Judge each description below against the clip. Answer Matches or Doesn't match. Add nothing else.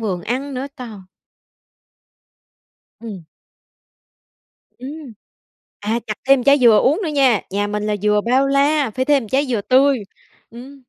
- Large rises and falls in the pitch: Doesn't match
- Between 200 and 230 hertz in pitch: Doesn't match